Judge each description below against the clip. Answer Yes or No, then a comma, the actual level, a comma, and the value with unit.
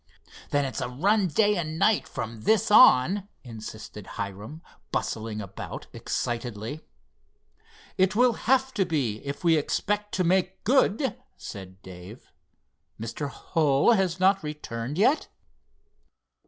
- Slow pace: Yes, slow, 125 wpm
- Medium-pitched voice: Yes, medium, 155 Hz